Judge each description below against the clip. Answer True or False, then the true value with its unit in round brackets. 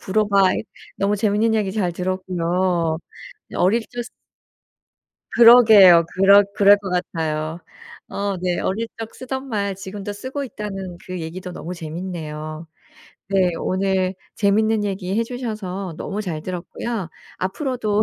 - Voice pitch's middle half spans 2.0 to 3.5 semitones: True (2.9 semitones)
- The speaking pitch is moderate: False (195 Hz)